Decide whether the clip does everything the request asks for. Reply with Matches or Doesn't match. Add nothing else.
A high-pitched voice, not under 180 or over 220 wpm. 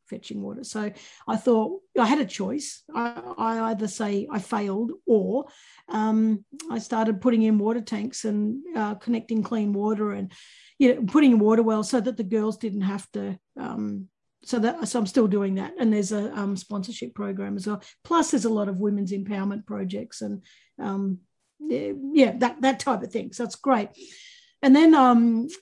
Matches